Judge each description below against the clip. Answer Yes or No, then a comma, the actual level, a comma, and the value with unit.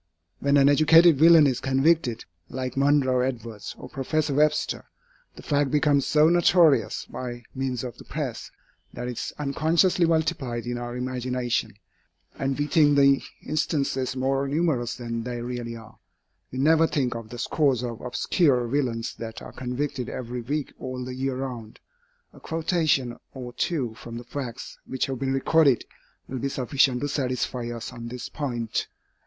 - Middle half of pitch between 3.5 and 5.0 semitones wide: No, average, 3.1 semitones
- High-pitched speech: No, low, 130 Hz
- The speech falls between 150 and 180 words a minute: Yes, average, 160 wpm